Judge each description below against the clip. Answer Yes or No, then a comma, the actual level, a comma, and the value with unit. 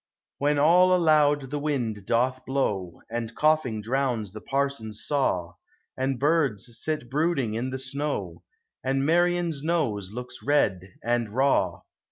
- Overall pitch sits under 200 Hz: Yes, low, 135 Hz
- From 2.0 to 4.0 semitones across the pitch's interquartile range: No, average, 4.6 semitones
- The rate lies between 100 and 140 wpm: Yes, slow, 135 wpm